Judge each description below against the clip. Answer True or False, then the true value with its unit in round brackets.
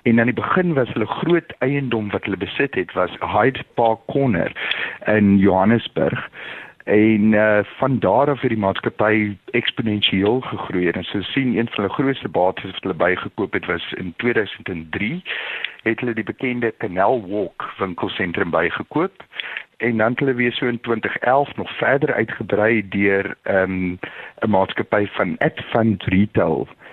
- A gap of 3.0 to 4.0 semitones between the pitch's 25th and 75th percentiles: True (3.5 semitones)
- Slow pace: False (160 wpm)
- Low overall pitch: True (110 Hz)